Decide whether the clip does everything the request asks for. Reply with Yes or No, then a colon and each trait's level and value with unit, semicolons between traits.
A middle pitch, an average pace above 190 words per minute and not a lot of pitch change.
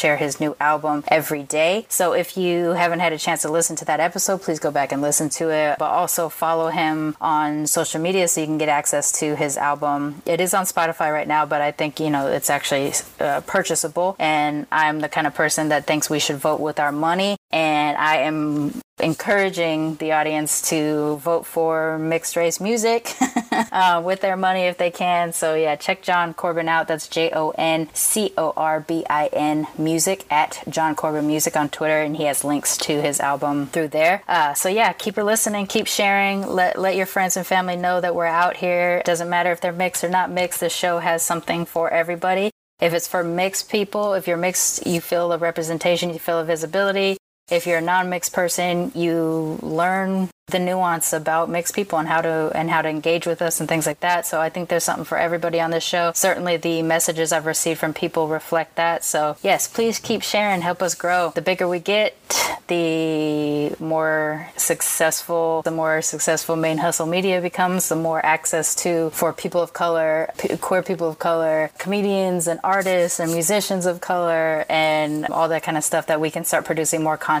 Yes: medium, 165 Hz; average, 200 wpm; narrow, 2.3 semitones